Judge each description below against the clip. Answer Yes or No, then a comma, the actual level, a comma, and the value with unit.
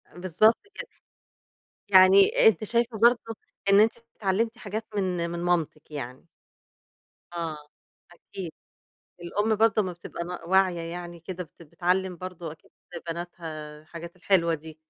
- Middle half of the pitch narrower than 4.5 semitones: Yes, average, 3.3 semitones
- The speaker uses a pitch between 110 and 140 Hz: No, medium, 180 Hz